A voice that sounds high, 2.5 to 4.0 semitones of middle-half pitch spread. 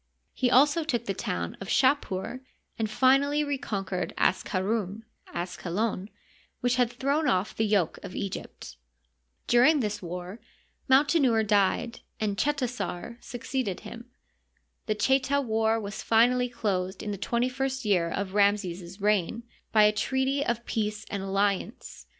No: high, 220 Hz; average, 4.6 semitones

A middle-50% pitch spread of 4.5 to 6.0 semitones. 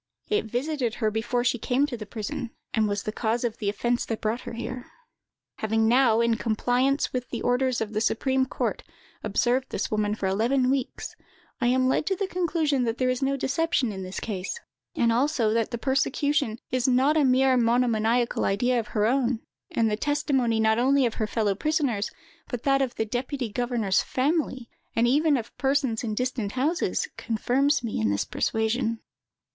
No: average, 3.2 semitones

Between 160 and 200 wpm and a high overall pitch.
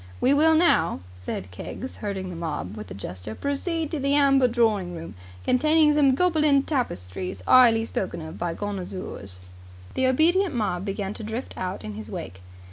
Yes: average, 170 wpm; high, 215 Hz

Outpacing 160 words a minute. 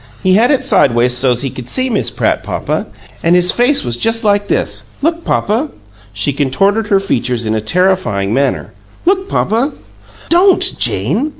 Yes: average, 170 wpm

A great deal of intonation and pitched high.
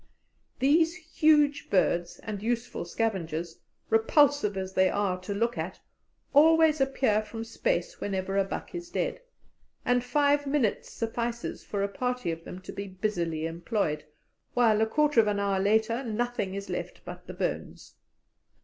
Yes: wide, 6.0 semitones; high, 220 Hz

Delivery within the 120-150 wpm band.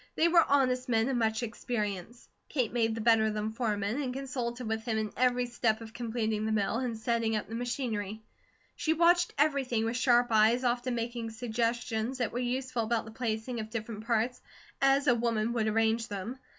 No: average, 195 wpm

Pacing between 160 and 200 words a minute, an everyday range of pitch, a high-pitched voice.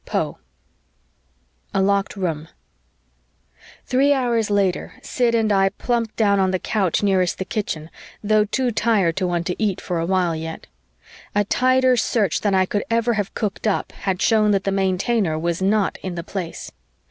Yes: average, 170 wpm; average, 3.3 semitones; high, 200 Hz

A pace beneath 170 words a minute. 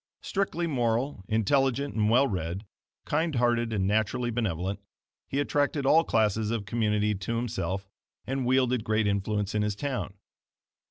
Yes: average, 145 wpm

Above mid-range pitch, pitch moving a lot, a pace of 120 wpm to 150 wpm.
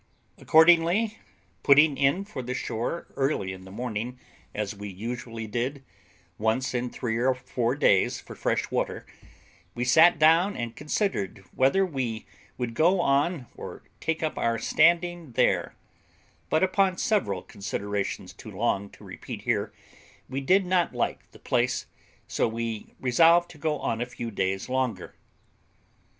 No: low, 130 Hz; wide, 6.2 semitones; average, 145 wpm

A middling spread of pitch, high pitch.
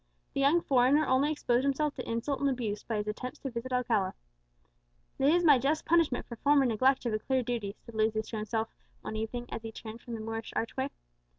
Yes: average, 3.6 semitones; high, 245 Hz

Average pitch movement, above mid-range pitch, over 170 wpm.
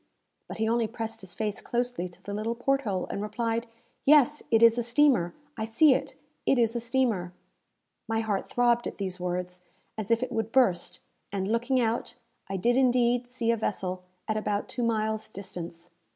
Yes: average, 3.3 semitones; high, 225 Hz; average, 190 wpm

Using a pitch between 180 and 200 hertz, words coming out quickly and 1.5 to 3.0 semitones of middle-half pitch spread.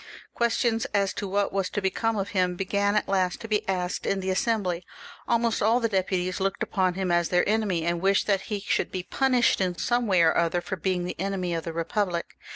Yes: high, 190 Hz; fast, 225 wpm; average, 2.7 semitones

